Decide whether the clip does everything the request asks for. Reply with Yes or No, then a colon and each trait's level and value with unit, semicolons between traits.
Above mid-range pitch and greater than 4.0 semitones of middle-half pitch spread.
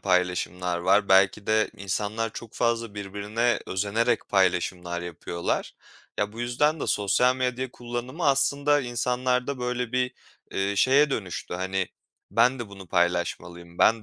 No: low, 110 Hz; average, 4.7 semitones